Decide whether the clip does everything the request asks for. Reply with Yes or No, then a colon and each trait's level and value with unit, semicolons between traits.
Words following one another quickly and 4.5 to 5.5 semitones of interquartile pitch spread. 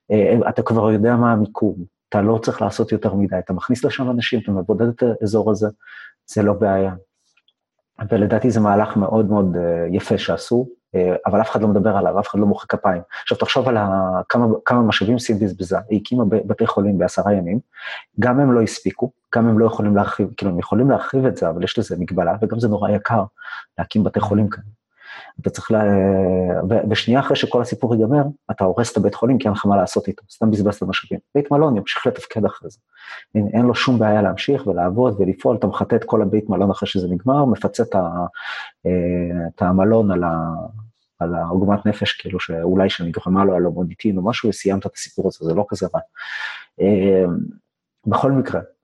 No: fast, 195 wpm; average, 3.2 semitones